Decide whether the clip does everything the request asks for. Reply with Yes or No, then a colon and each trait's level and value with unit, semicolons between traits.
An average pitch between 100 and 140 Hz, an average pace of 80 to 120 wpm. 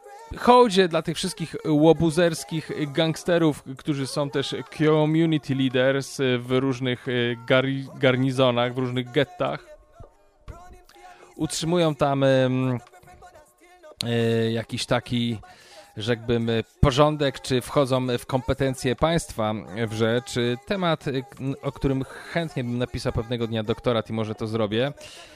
Yes: low, 135 Hz; slow, 110 wpm